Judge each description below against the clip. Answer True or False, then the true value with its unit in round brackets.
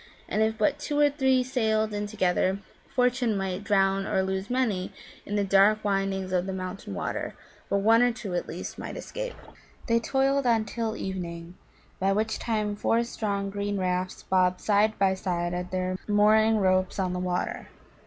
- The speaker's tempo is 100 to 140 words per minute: False (180 wpm)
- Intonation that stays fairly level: False (3.0 semitones)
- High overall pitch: True (200 Hz)